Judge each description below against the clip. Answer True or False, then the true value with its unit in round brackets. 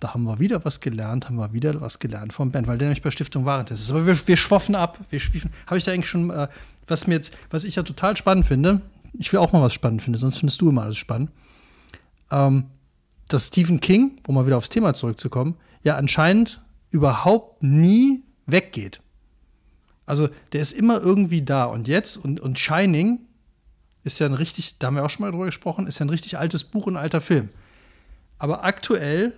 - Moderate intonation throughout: False (6.4 semitones)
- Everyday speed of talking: False (215 wpm)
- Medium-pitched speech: True (150 Hz)